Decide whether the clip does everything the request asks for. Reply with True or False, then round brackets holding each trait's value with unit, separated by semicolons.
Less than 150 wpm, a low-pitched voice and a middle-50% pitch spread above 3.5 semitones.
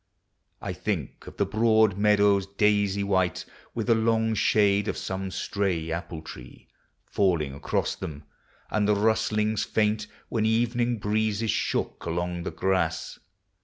False (140 wpm; 100 Hz; 2.9 semitones)